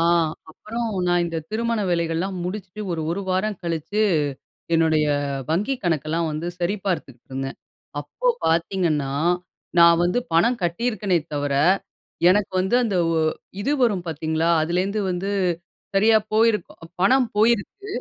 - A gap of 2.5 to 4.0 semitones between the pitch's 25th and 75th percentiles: No, average, 4.5 semitones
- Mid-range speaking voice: Yes, medium, 180 Hz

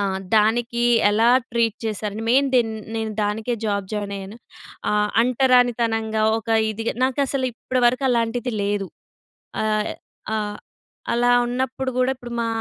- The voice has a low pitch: No, high, 230 Hz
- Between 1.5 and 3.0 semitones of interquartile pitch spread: Yes, narrow, 2.5 semitones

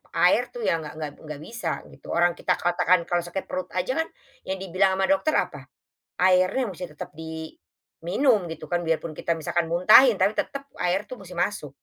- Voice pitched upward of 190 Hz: No, medium, 180 Hz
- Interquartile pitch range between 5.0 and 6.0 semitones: No, average, 2.9 semitones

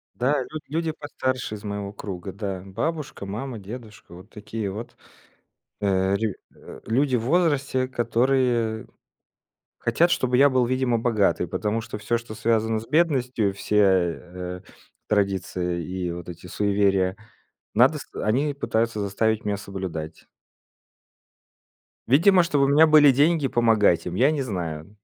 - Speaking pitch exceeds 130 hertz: No, low, 110 Hz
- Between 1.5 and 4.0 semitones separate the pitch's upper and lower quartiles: No, average, 5.0 semitones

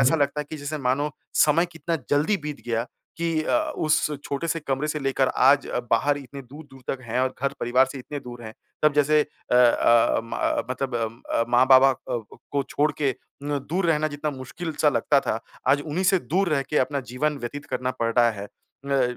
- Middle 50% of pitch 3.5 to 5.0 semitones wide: No, average, 2.9 semitones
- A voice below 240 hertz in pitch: Yes, medium, 140 Hz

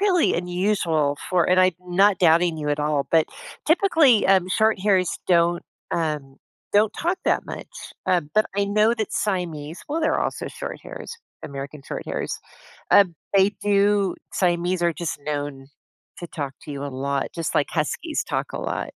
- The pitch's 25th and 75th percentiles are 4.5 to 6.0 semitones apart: Yes, average, 5.1 semitones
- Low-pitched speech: No, medium, 175 Hz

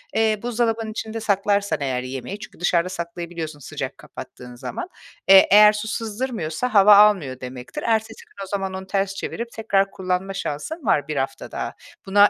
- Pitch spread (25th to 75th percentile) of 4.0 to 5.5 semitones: Yes, average, 4.5 semitones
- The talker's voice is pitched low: No, high, 195 Hz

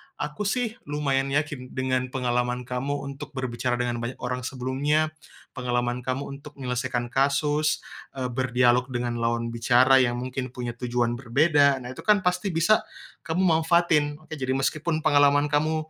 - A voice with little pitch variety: No, average, 3.2 semitones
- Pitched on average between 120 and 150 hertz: Yes, low, 135 Hz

